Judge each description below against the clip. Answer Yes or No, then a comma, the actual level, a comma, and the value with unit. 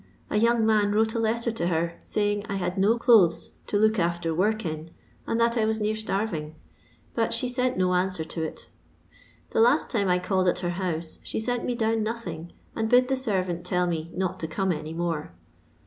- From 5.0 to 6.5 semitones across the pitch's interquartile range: No, average, 4.4 semitones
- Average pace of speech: No, fast, 210 wpm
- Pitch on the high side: Yes, high, 195 Hz